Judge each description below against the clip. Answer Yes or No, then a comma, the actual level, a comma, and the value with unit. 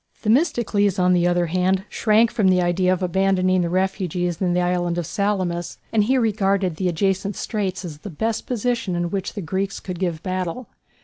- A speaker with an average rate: Yes, average, 190 wpm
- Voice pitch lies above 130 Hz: Yes, medium, 185 Hz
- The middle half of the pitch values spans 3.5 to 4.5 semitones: No, narrow, 2.4 semitones